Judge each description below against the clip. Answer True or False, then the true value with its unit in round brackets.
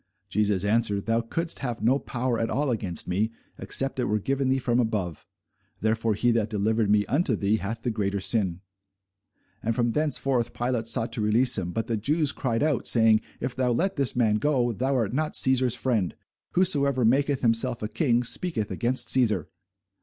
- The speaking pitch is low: True (115 Hz)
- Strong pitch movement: False (3.4 semitones)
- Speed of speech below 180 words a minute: False (185 wpm)